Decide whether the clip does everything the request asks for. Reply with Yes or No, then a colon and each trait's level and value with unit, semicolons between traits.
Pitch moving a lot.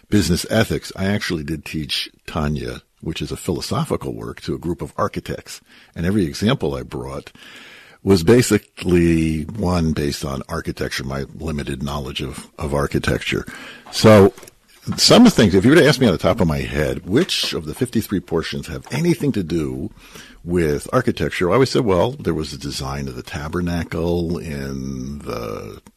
No: average, 4.7 semitones